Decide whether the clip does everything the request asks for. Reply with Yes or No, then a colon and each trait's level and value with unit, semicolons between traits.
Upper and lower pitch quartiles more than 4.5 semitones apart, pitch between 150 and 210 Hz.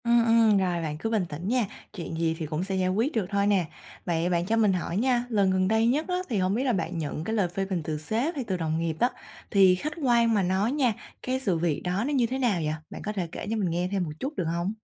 Yes: average, 5.0 semitones; high, 195 Hz